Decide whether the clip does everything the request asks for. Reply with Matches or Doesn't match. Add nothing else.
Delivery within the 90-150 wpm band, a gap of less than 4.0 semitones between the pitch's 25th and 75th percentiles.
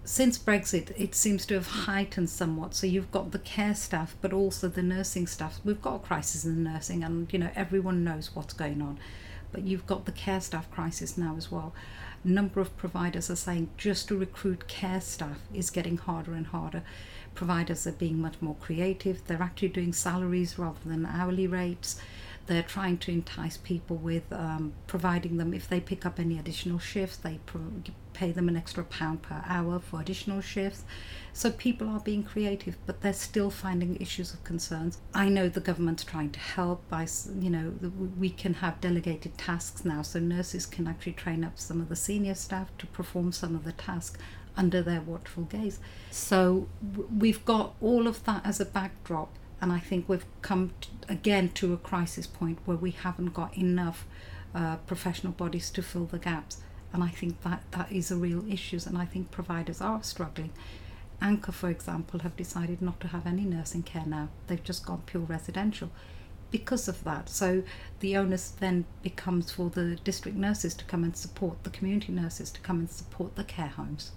Doesn't match